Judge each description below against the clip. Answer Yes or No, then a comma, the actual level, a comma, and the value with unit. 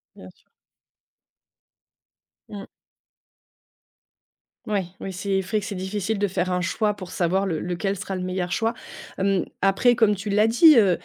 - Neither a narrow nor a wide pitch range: No, narrow, 2.3 semitones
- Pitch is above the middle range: Yes, high, 195 Hz